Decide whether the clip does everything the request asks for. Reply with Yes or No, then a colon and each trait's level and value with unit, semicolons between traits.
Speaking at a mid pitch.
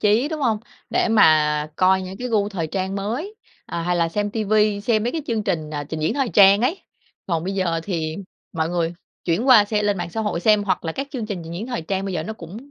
No: high, 195 Hz